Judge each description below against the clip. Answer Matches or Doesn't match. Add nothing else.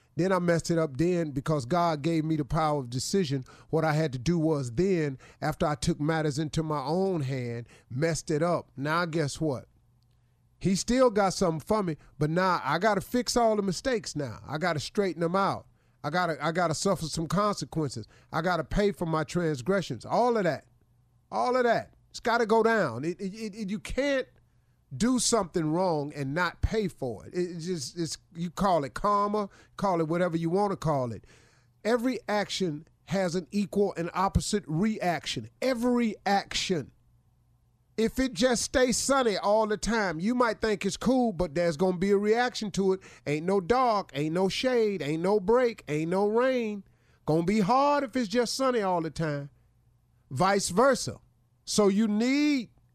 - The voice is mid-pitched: Matches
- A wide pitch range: Matches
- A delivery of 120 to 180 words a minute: Doesn't match